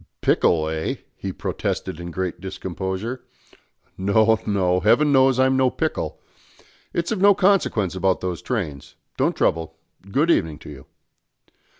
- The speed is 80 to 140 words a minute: Yes, slow, 135 wpm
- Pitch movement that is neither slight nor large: No, wide, 7.2 semitones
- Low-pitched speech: Yes, very low, 95 Hz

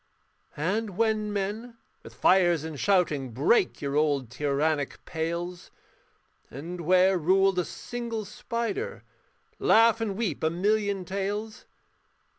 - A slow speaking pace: Yes, slow, 115 wpm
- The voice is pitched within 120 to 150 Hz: No, high, 190 Hz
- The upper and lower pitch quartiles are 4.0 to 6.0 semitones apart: Yes, average, 5.1 semitones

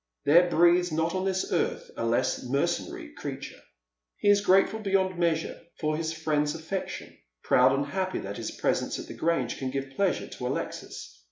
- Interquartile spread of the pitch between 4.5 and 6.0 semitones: Yes, average, 4.9 semitones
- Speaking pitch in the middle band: Yes, medium, 165 Hz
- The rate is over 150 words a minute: Yes, average, 175 wpm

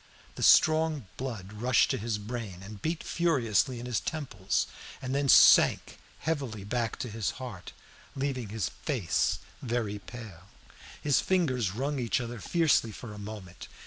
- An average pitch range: Yes, average, 4.5 semitones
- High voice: No, low, 120 Hz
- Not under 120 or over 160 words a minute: Yes, average, 150 wpm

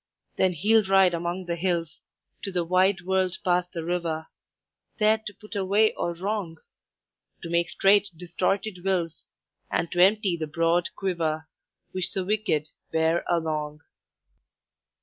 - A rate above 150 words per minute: No, average, 140 wpm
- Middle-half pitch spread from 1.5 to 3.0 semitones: Yes, narrow, 2.6 semitones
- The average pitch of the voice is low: No, medium, 180 Hz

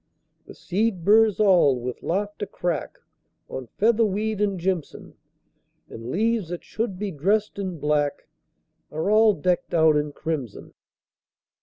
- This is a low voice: No, medium, 185 Hz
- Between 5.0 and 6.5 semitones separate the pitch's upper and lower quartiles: Yes, wide, 5.4 semitones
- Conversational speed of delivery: No, slow, 130 wpm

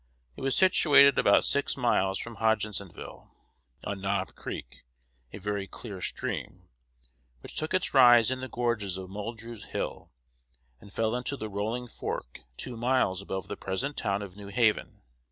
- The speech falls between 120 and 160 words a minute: Yes, average, 155 wpm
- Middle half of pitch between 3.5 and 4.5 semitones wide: Yes, average, 3.8 semitones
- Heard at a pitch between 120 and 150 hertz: No, low, 110 Hz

